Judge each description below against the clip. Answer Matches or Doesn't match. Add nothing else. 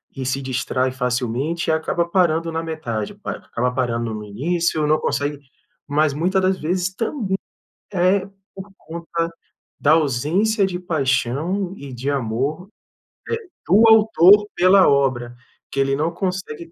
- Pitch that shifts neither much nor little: Doesn't match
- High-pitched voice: Doesn't match